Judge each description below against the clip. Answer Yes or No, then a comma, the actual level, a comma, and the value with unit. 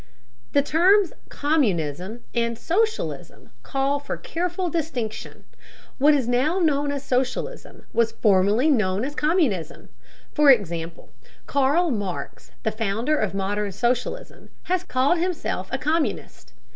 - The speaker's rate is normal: No, slow, 120 wpm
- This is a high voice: Yes, very high, 265 Hz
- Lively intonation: Yes, wide, 6.7 semitones